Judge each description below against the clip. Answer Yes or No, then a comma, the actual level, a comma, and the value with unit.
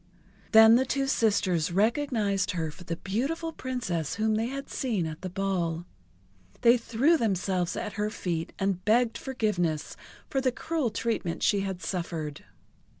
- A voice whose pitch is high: Yes, high, 205 Hz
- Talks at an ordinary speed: Yes, average, 150 wpm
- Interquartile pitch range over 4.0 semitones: Yes, average, 5.3 semitones